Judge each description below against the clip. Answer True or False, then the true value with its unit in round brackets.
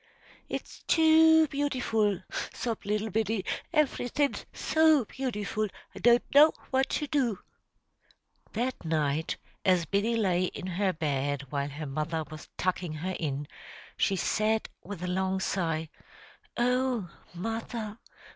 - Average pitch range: False (6.5 semitones)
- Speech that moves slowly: True (125 wpm)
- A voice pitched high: True (205 Hz)